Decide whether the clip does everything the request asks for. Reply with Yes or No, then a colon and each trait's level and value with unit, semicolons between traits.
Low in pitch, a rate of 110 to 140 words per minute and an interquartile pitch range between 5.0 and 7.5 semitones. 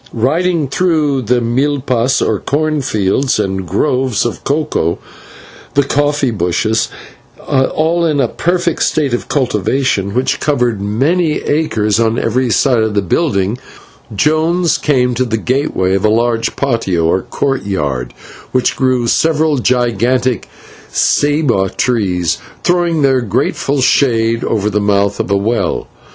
Yes: low, 125 Hz; slow, 135 wpm; wide, 5.5 semitones